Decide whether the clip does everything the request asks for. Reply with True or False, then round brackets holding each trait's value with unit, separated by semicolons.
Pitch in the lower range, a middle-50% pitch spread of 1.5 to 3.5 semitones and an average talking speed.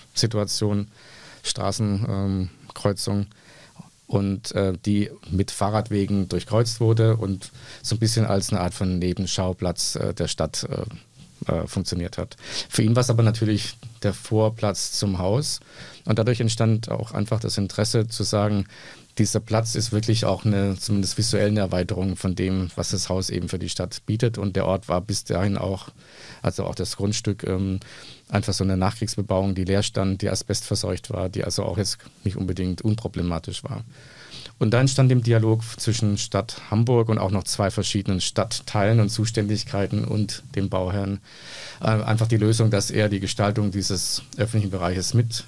True (105 Hz; 2.5 semitones; 165 wpm)